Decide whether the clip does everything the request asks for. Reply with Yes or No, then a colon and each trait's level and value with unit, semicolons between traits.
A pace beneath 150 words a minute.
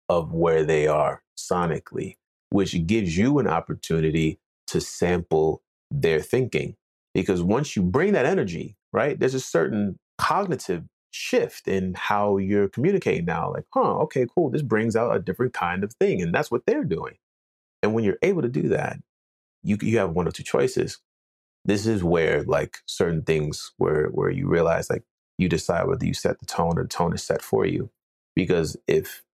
No: average, 180 wpm